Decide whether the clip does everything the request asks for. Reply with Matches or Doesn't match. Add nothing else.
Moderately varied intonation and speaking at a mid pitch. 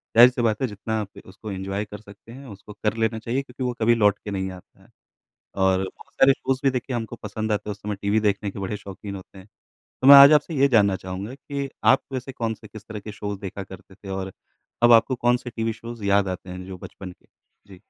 Doesn't match